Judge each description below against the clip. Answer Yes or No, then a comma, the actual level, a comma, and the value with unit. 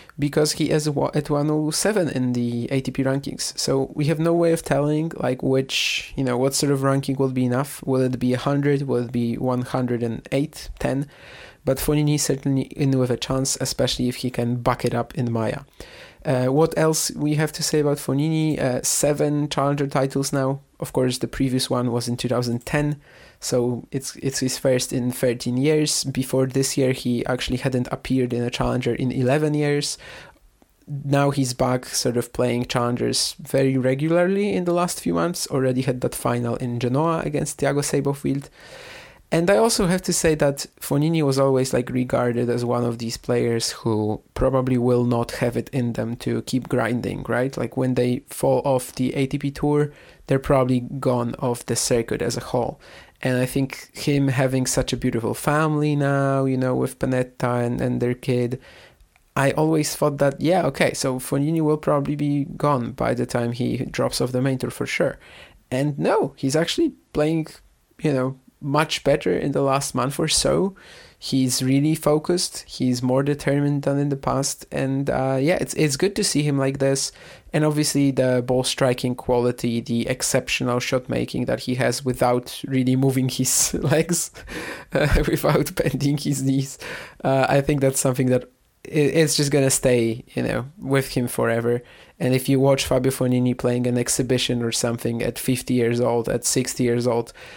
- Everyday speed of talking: Yes, average, 185 wpm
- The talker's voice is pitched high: No, low, 135 Hz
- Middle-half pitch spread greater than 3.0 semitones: No, narrow, 2.6 semitones